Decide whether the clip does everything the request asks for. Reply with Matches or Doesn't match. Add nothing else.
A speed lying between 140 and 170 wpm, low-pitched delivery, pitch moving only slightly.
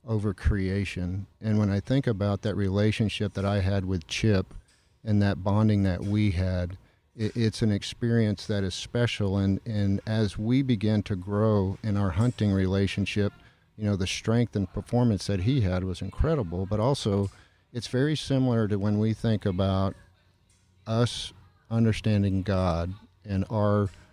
Matches